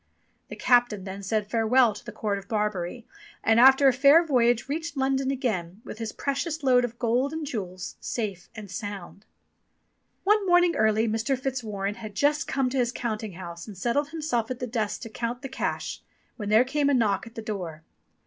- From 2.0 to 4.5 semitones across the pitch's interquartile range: Yes, average, 4.2 semitones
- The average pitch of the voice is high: Yes, high, 235 Hz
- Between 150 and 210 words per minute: Yes, average, 195 wpm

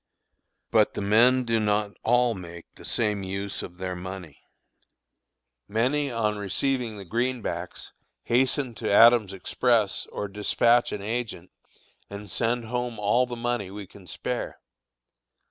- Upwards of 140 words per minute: No, slow, 135 wpm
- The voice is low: Yes, low, 110 Hz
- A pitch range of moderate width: Yes, average, 3.5 semitones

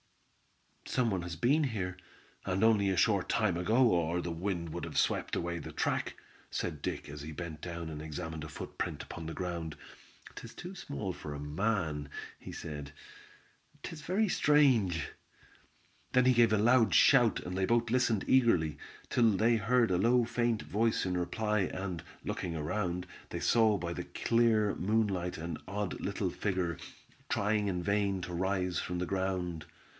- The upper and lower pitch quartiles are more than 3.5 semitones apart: Yes, average, 4.9 semitones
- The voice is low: Yes, very low, 95 Hz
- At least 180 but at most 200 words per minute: No, average, 170 wpm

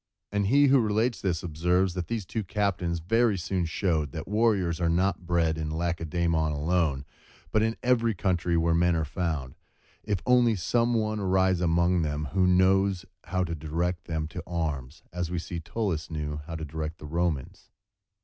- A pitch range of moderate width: Yes, average, 3.5 semitones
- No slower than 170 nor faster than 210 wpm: Yes, average, 180 wpm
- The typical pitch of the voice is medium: No, very low, 85 Hz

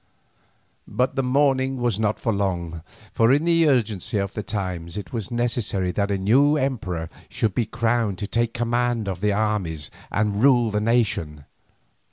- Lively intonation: No, average, 3.7 semitones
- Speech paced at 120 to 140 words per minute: No, average, 170 wpm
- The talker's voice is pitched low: Yes, low, 110 Hz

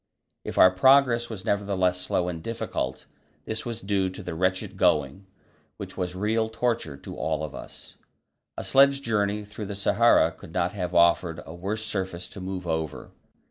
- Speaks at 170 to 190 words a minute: Yes, average, 175 wpm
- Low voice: Yes, very low, 95 Hz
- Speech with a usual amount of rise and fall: Yes, average, 3.9 semitones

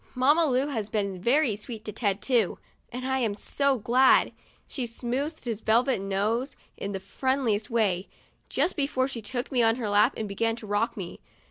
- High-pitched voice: Yes, high, 230 Hz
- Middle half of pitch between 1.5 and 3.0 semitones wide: No, average, 4.0 semitones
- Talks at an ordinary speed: Yes, average, 185 wpm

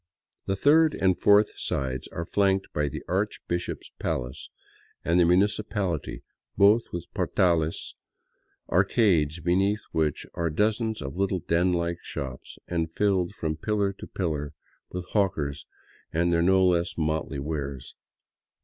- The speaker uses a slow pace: Yes, slow, 130 wpm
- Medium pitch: No, very low, 85 Hz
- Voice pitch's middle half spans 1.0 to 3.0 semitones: No, average, 3.9 semitones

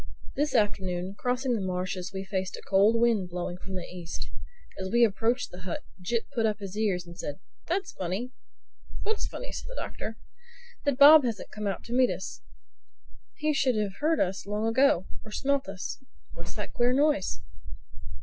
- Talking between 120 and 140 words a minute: No, average, 180 wpm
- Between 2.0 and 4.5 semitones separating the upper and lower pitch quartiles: No, average, 5.3 semitones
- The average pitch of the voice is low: No, high, 210 Hz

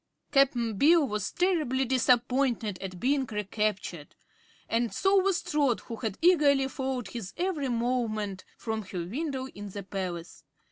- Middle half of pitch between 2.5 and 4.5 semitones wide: No, average, 5.2 semitones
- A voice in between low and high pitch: No, high, 240 Hz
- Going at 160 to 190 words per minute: No, average, 140 wpm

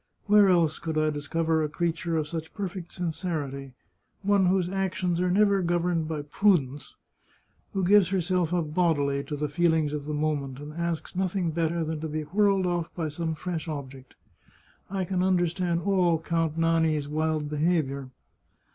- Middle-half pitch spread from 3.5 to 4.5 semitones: No, average, 2.9 semitones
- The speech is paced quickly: No, average, 165 wpm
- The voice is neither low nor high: Yes, medium, 165 Hz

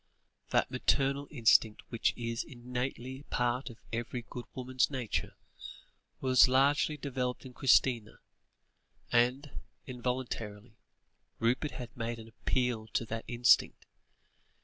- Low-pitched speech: Yes, low, 125 Hz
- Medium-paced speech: No, slow, 110 wpm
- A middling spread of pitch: No, narrow, 2.0 semitones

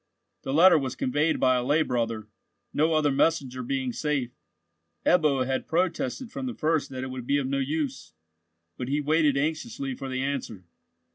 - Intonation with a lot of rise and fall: No, average, 3.6 semitones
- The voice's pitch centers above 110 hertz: Yes, medium, 140 Hz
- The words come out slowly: No, average, 170 wpm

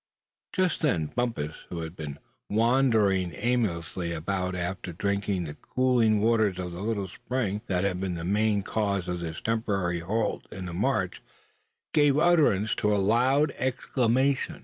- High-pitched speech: No, low, 100 Hz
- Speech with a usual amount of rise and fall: Yes, average, 4.9 semitones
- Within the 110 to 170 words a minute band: Yes, average, 155 wpm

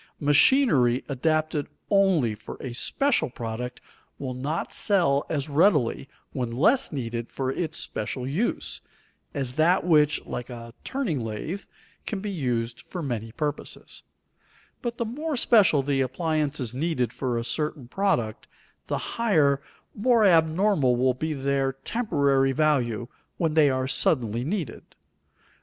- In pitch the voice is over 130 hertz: Yes, medium, 140 Hz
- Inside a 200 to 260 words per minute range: No, slow, 135 wpm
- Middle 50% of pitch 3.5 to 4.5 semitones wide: No, wide, 5.4 semitones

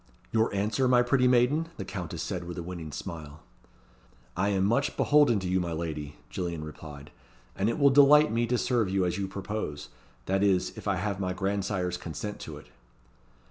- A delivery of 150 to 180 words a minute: No, average, 190 wpm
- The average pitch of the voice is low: Yes, very low, 95 Hz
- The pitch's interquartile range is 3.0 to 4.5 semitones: No, average, 5.1 semitones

